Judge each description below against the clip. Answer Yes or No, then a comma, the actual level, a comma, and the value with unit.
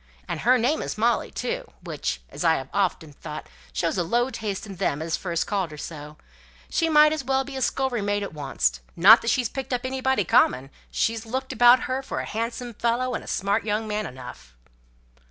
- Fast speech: Yes, fast, 210 wpm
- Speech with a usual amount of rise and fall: No, wide, 7.3 semitones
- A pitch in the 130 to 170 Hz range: No, high, 220 Hz